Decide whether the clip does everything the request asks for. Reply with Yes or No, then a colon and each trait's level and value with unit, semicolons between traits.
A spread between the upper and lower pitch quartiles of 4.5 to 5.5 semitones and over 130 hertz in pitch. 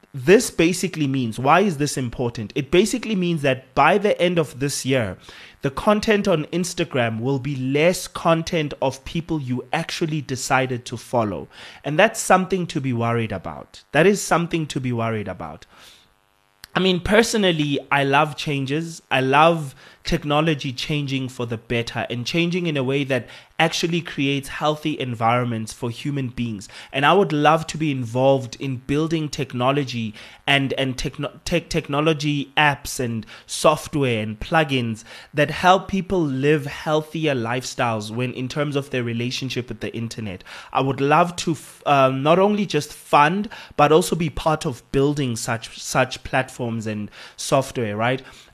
Yes: average, 4.8 semitones; medium, 140 Hz